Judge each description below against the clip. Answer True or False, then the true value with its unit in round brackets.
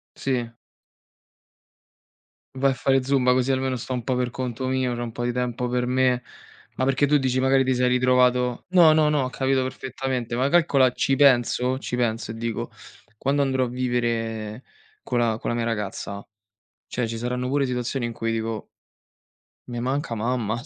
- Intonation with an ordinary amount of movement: False (1.8 semitones)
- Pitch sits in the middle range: False (125 Hz)